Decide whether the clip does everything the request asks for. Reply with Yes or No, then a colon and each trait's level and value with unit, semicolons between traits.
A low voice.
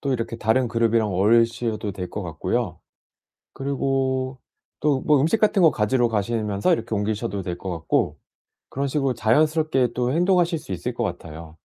Yes: low, 120 Hz